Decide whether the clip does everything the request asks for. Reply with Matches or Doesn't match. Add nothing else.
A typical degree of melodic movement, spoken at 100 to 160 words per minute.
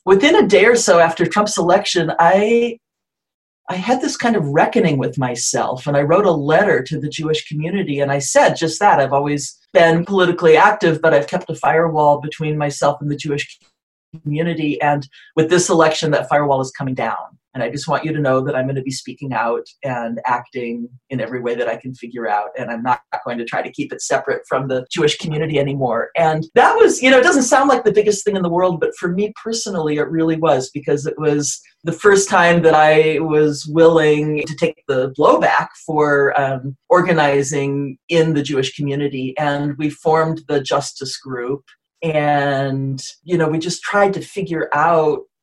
Doesn't match